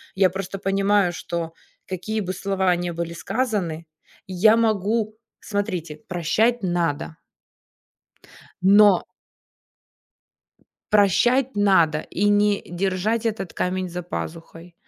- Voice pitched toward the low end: No, high, 190 Hz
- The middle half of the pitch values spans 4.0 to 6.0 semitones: No, average, 3.1 semitones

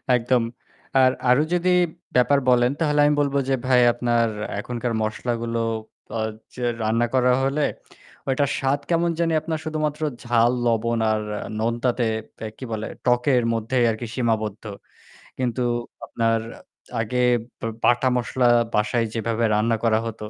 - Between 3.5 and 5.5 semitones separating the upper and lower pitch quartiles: No, narrow, 2.5 semitones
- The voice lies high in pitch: No, low, 120 Hz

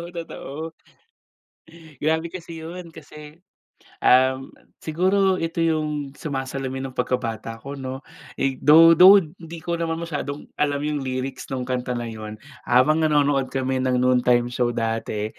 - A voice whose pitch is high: No, medium, 140 Hz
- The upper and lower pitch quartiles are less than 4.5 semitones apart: Yes, average, 4.1 semitones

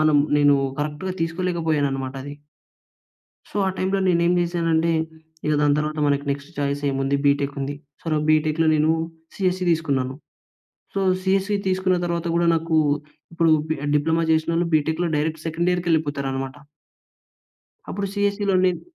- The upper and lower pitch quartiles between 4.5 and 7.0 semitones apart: No, average, 3.3 semitones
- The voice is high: No, medium, 160 Hz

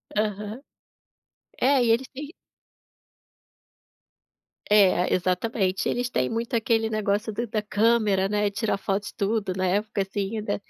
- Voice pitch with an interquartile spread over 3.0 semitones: No, narrow, 2.4 semitones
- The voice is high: Yes, high, 210 Hz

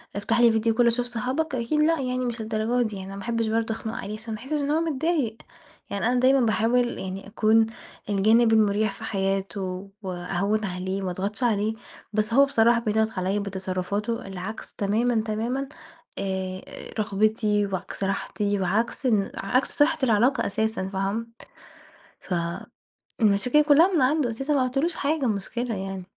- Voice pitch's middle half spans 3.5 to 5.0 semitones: Yes, average, 3.8 semitones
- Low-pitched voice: No, high, 220 Hz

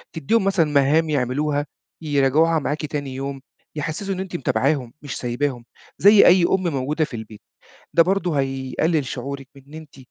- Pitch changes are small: No, average, 3.3 semitones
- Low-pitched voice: No, medium, 145 Hz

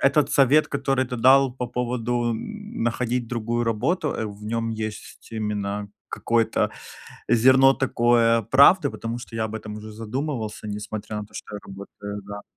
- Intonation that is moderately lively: Yes, average, 3.5 semitones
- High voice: No, low, 115 Hz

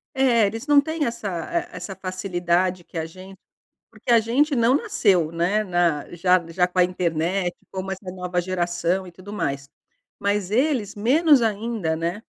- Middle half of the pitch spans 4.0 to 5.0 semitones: Yes, average, 4.3 semitones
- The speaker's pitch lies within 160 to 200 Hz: Yes, high, 190 Hz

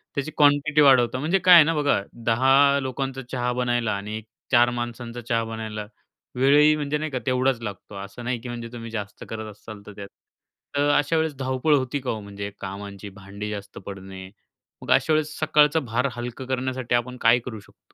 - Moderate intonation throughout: Yes, average, 4.3 semitones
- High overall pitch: No, low, 125 Hz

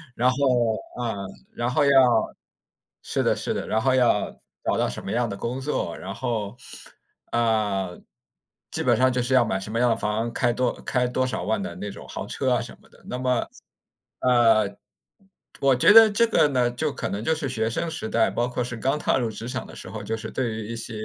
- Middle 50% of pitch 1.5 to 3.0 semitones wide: Yes, average, 2.7 semitones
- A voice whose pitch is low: Yes, low, 120 Hz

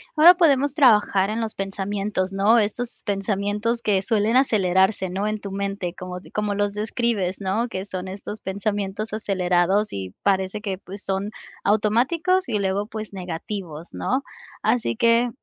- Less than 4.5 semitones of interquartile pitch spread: Yes, narrow, 2.6 semitones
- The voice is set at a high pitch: Yes, high, 205 Hz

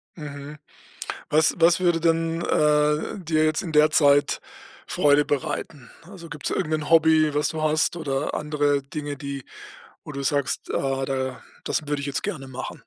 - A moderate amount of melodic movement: No, narrow, 2.0 semitones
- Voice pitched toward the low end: No, medium, 150 Hz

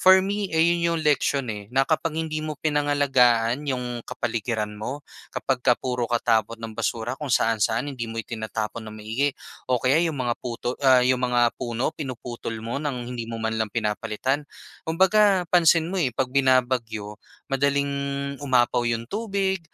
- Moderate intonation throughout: Yes, average, 4.2 semitones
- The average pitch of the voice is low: Yes, low, 130 Hz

